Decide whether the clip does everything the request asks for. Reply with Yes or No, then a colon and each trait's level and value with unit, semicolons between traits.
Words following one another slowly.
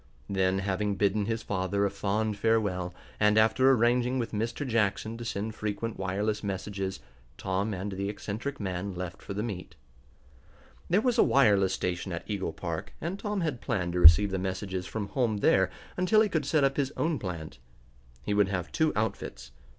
No: average, 180 wpm